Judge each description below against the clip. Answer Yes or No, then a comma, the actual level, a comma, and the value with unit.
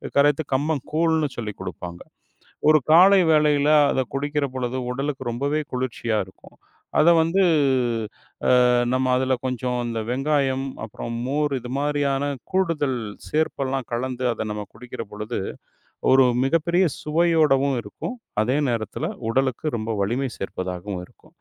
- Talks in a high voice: No, low, 135 Hz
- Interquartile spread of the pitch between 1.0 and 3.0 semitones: No, average, 4.0 semitones